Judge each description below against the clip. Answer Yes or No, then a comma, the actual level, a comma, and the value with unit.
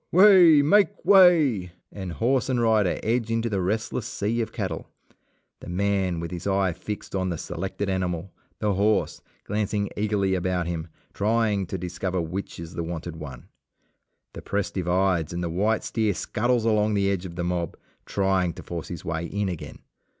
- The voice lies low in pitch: Yes, very low, 95 Hz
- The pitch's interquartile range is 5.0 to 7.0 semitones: No, average, 3.7 semitones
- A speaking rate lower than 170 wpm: No, average, 175 wpm